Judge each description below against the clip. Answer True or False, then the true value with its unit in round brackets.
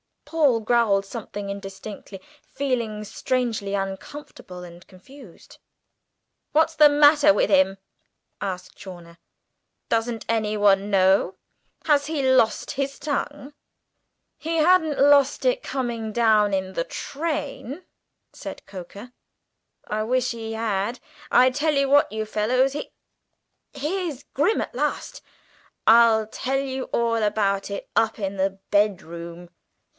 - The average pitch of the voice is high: True (230 Hz)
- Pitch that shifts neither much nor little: False (6.0 semitones)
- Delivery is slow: True (120 wpm)